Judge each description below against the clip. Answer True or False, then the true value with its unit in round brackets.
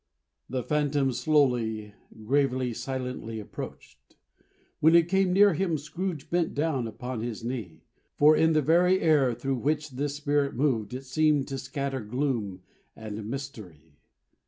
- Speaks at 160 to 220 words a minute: False (140 wpm)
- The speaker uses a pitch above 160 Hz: False (135 Hz)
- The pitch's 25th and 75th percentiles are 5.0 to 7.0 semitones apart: False (4.5 semitones)